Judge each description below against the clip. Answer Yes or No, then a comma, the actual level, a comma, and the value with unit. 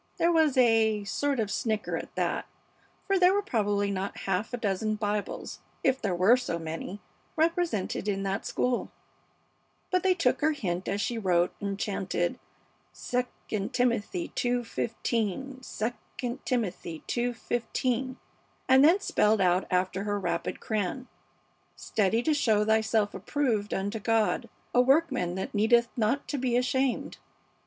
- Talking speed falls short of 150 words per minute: Yes, average, 140 wpm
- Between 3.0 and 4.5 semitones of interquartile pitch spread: Yes, average, 4.2 semitones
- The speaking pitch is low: No, high, 225 Hz